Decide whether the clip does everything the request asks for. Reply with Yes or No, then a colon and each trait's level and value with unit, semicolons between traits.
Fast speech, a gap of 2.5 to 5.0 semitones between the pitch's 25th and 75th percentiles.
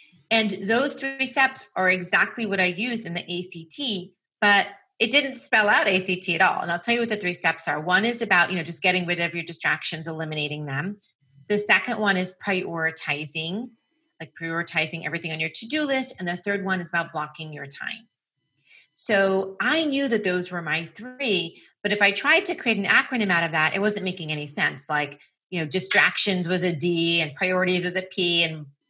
Yes: fast, 210 wpm; average, 4.2 semitones